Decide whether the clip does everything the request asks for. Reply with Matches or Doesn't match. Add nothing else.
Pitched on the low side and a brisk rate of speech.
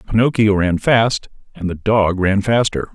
Doesn't match